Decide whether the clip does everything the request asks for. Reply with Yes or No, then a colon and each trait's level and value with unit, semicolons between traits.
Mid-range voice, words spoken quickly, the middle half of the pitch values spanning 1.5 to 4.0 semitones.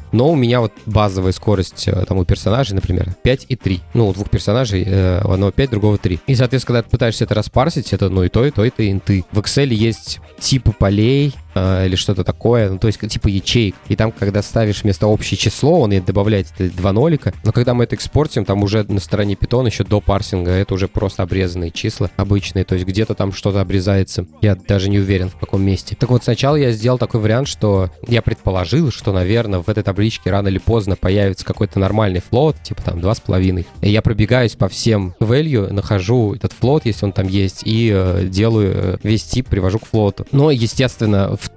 No: low, 105 Hz; fast, 215 wpm; average, 3.3 semitones